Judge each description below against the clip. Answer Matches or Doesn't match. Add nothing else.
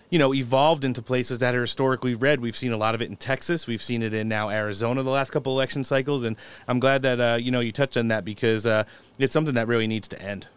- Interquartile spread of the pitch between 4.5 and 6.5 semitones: Doesn't match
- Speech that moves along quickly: Matches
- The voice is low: Matches